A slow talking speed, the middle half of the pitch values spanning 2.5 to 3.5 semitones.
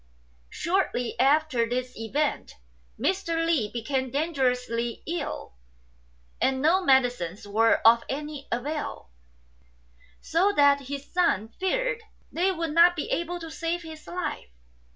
No: slow, 120 wpm; wide, 5.4 semitones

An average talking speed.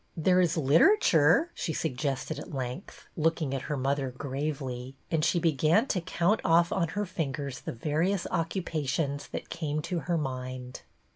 Yes: average, 155 wpm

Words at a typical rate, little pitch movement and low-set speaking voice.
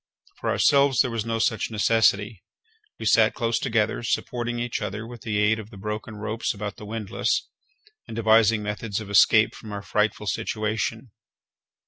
Yes: average, 165 wpm; narrow, 1.5 semitones; low, 110 Hz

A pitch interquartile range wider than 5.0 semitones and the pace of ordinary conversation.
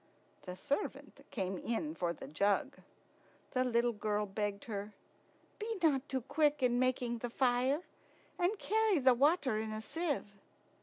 Yes: wide, 5.6 semitones; average, 150 wpm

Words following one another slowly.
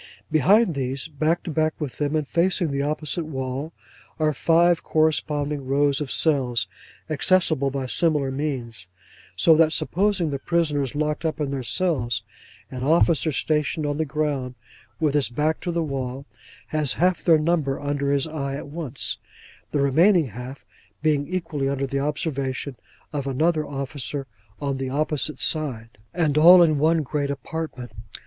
No: average, 155 wpm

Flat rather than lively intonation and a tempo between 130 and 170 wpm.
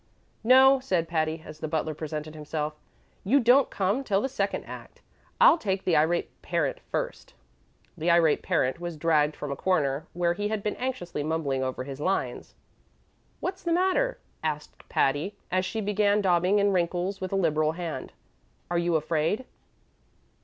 No: average, 4.9 semitones; average, 165 wpm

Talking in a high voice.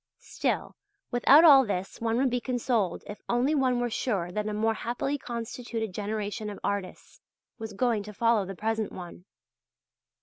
Yes: high, 225 Hz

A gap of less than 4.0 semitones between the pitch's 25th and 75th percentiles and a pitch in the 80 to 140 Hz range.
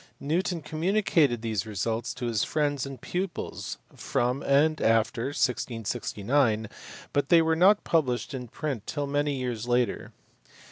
No: average, 4.9 semitones; low, 135 Hz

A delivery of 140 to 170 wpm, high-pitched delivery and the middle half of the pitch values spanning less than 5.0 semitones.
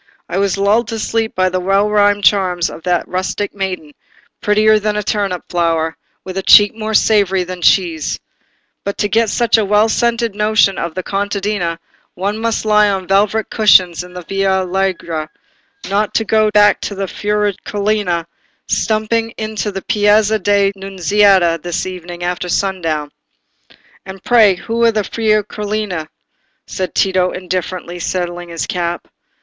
Yes: average, 155 wpm; high, 195 Hz; average, 2.7 semitones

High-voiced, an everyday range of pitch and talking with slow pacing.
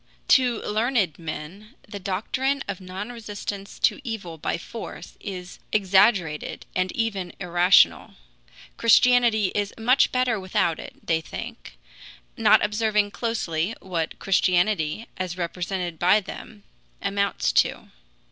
Yes: high, 200 Hz; average, 3.8 semitones; slow, 120 wpm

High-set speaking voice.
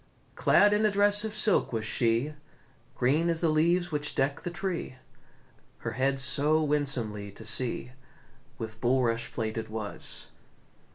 No: low, 135 Hz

